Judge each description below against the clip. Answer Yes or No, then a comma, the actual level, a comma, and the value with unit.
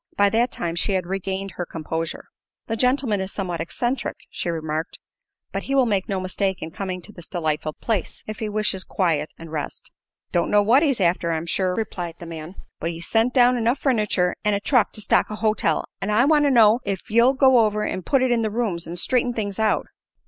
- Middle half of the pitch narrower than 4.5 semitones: No, average, 5.1 semitones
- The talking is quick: Yes, fast, 220 wpm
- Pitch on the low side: No, high, 200 Hz